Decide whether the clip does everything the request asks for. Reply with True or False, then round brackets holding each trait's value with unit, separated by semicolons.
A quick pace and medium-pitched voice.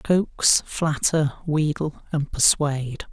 False (95 wpm; 150 Hz)